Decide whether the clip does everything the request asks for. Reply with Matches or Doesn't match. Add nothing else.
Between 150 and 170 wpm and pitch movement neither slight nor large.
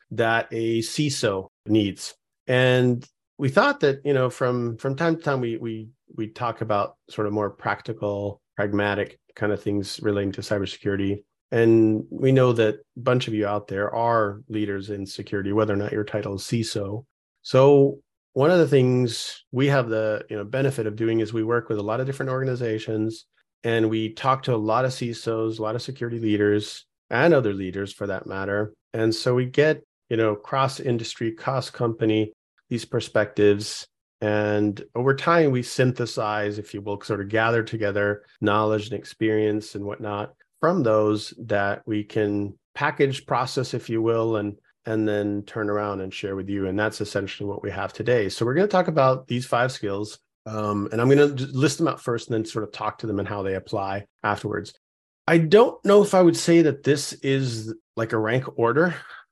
Doesn't match